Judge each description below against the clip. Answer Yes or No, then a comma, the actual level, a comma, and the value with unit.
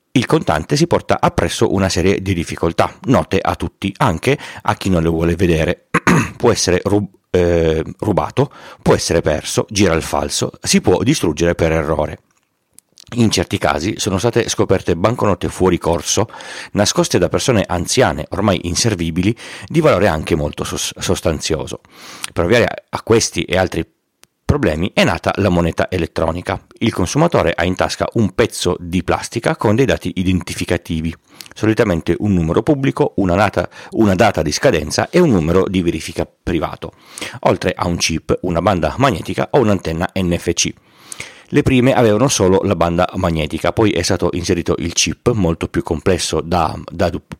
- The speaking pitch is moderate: No, very low, 90 Hz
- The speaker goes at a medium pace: Yes, average, 160 wpm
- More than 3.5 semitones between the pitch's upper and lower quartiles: No, average, 3.1 semitones